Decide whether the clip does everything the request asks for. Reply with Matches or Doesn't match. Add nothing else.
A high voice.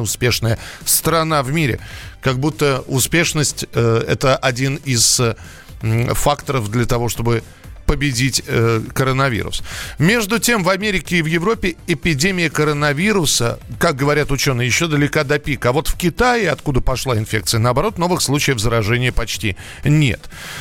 Doesn't match